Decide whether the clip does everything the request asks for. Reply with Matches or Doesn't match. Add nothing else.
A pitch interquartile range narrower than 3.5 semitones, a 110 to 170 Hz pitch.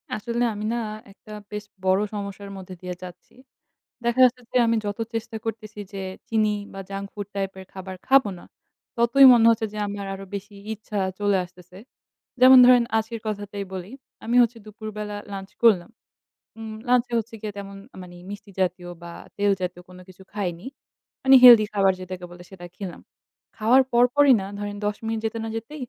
Doesn't match